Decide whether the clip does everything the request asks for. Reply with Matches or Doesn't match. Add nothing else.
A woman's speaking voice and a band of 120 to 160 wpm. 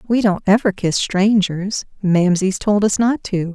Matches